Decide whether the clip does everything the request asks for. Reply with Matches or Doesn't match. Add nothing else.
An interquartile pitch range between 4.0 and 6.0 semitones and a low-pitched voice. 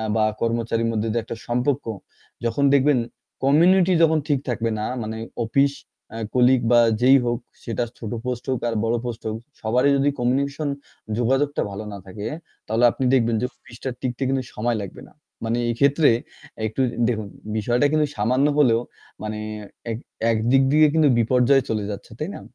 Doesn't match